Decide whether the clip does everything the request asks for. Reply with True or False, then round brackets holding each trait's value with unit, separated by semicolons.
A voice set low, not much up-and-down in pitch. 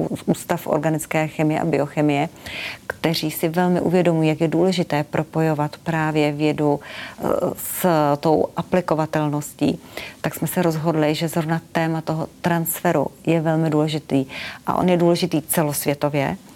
False (160 Hz; 2.0 semitones)